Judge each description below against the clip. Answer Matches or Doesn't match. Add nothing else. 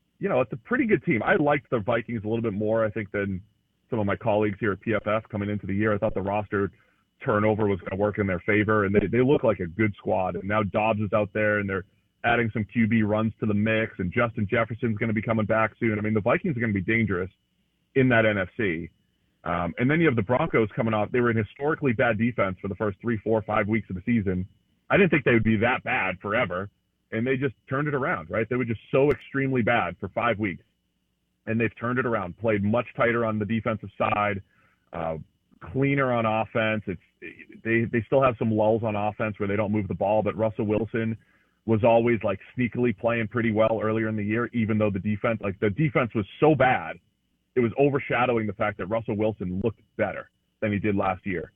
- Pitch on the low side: Matches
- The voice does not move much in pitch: Matches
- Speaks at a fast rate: Matches